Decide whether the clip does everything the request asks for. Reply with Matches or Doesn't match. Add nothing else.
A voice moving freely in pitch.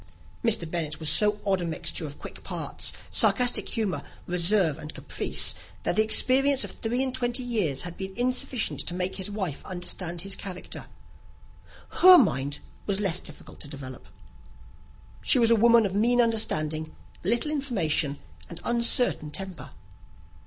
Matches